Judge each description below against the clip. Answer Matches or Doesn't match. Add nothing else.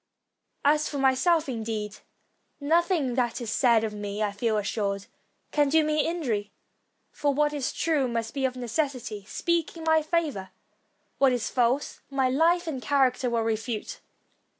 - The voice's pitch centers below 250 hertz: Doesn't match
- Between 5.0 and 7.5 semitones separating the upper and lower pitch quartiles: Matches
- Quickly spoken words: Doesn't match